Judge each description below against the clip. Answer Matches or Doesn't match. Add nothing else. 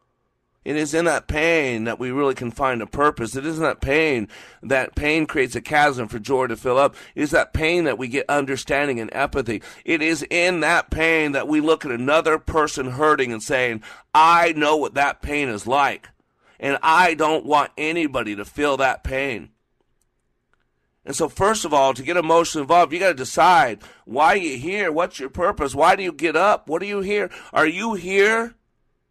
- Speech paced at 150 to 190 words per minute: Doesn't match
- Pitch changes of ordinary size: Matches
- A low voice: Doesn't match